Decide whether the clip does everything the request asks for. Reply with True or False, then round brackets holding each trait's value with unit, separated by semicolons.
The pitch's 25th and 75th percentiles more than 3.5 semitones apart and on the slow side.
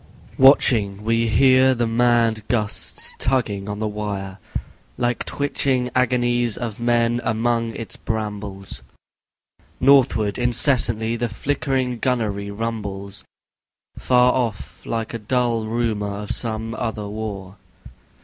False (2.7 semitones; 110 wpm)